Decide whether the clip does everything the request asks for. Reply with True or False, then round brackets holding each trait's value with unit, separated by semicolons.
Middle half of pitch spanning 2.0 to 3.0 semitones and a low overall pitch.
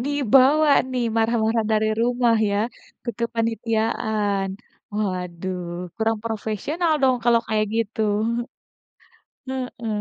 False (2.4 semitones; 225 Hz)